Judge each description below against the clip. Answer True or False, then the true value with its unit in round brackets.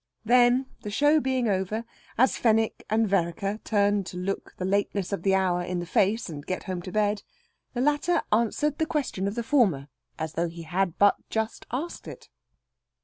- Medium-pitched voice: False (205 Hz)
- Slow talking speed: False (190 wpm)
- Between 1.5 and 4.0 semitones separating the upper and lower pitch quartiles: False (4.5 semitones)